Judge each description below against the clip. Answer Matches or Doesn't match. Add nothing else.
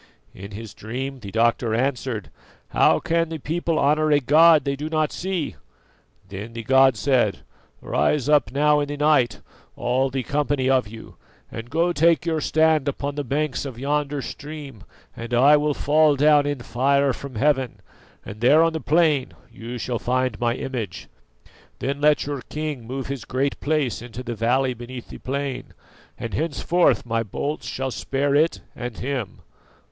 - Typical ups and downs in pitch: Matches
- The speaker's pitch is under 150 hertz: Matches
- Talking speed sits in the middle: Matches